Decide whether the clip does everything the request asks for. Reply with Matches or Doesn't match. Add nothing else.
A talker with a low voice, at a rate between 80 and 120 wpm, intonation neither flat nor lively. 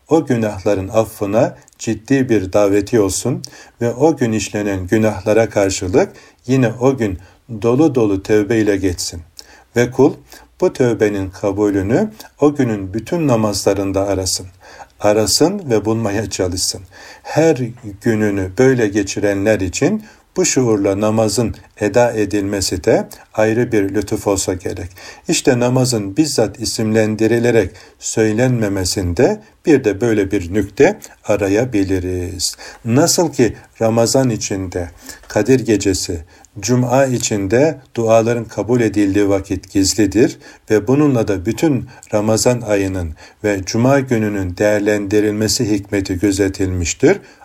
Matches